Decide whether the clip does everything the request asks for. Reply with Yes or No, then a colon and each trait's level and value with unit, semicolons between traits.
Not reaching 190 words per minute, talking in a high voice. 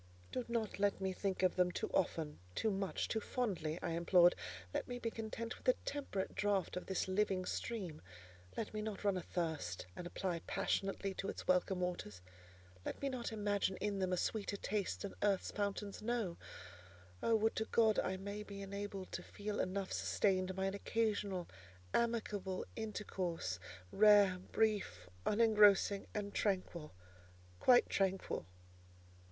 Yes: average, 155 wpm; high, 200 Hz